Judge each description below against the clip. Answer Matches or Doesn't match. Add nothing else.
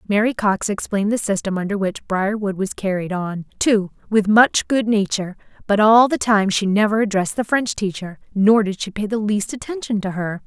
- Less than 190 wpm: Doesn't match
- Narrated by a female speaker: Matches